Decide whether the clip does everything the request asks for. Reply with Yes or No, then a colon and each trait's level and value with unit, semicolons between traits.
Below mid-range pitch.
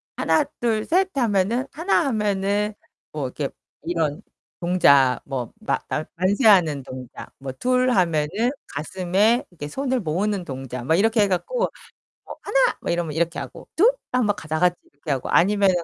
No: medium, 185 Hz